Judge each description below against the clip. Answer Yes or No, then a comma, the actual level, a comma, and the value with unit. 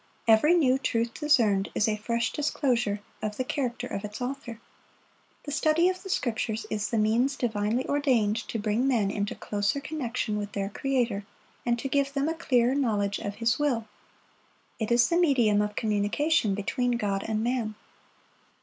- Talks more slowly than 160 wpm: No, average, 170 wpm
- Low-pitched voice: No, high, 235 Hz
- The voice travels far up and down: No, average, 4.5 semitones